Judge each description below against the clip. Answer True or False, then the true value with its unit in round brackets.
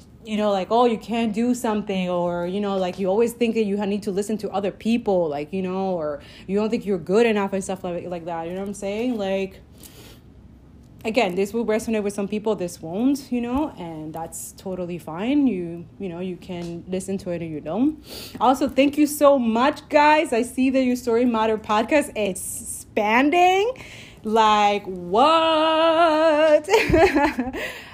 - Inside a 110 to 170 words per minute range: False (185 wpm)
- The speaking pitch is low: False (215 Hz)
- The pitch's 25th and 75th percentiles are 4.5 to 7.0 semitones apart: True (5.2 semitones)